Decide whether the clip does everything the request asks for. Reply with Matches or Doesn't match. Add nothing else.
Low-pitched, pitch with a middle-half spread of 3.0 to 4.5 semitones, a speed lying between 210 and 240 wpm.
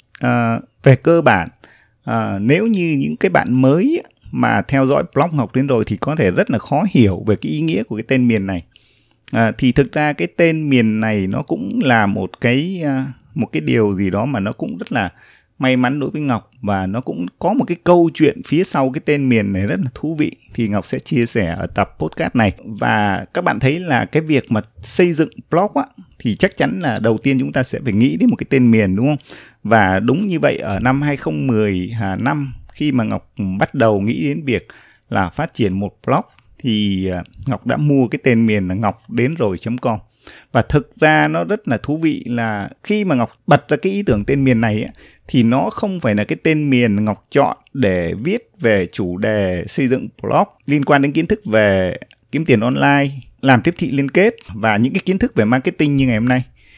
Doesn't match